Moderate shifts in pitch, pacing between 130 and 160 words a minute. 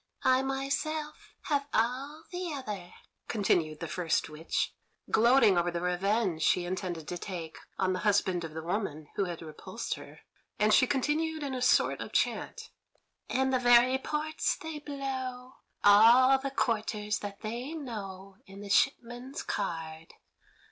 No: wide, 6.5 semitones; average, 150 wpm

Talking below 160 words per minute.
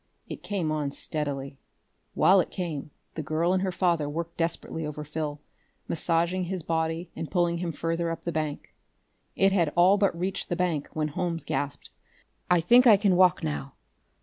No: average, 175 wpm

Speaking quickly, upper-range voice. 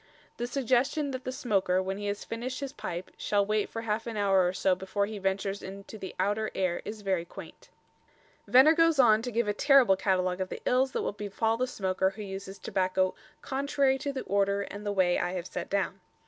Yes: fast, 215 wpm; high, 205 Hz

